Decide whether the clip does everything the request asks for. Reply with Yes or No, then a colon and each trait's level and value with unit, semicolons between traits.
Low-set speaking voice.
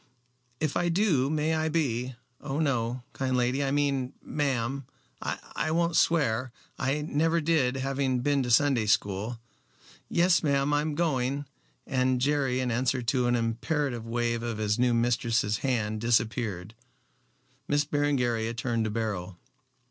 Yes: low, 130 Hz